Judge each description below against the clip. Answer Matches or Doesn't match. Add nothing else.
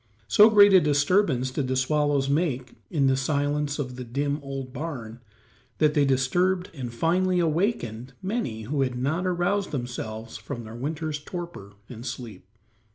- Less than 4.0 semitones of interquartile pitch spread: Doesn't match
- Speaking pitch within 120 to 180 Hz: Matches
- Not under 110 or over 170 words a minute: Matches